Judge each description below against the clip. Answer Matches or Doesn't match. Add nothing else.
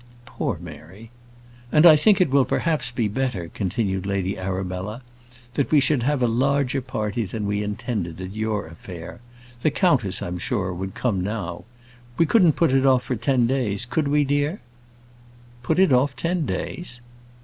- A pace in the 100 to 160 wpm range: Doesn't match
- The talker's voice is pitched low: Matches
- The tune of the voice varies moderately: Doesn't match